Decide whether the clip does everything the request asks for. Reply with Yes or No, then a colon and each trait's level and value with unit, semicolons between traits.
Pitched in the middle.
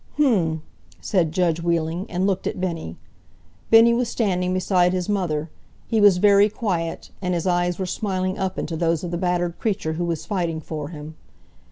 Yes: medium, 180 Hz